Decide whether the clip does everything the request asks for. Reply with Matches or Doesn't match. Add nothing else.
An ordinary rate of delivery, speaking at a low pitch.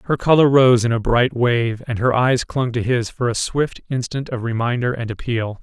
Doesn't match